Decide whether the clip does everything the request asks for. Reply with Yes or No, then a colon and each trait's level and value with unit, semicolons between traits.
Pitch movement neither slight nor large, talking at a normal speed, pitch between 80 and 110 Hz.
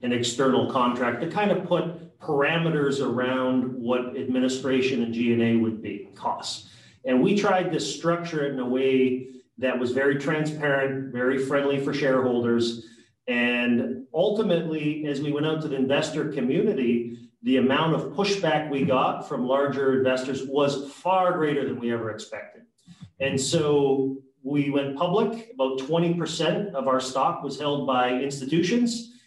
No: average, 3.4 semitones; average, 150 wpm; low, 135 Hz